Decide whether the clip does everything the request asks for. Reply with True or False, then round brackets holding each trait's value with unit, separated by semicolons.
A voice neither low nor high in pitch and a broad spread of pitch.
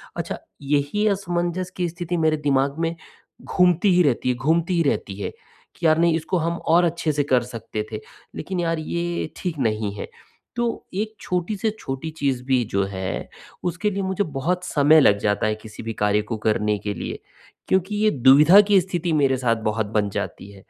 True (155 Hz; 6.5 semitones)